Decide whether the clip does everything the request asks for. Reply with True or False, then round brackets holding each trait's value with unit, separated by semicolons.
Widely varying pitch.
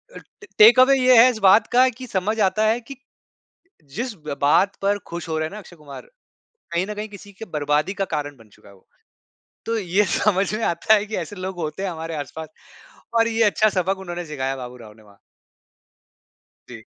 True (5.8 semitones)